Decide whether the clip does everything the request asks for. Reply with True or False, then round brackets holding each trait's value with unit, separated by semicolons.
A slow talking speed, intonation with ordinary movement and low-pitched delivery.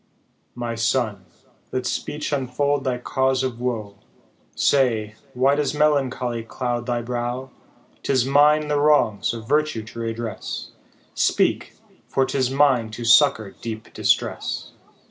True (130 wpm; 3.2 semitones; 125 Hz)